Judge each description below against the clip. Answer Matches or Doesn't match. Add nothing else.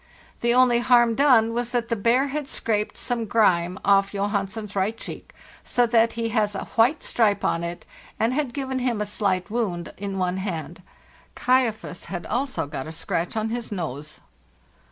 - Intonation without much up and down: Doesn't match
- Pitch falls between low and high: Doesn't match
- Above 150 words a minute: Matches